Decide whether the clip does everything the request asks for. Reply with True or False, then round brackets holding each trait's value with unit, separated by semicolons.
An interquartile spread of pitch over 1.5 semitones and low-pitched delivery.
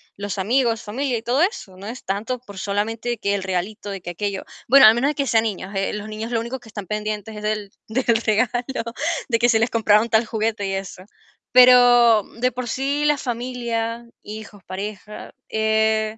False (2.7 semitones; 220 Hz)